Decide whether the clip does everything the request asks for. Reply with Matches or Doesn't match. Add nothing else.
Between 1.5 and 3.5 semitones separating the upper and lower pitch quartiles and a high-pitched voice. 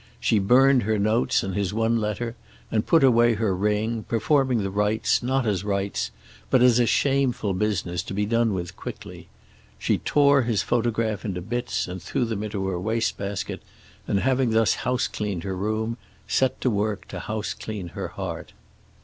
Doesn't match